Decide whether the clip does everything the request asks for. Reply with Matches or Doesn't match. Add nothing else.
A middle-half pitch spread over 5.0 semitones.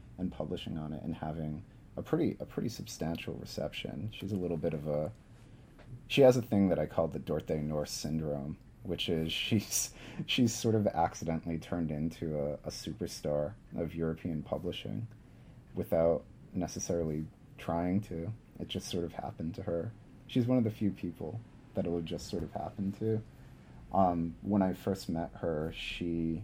Matches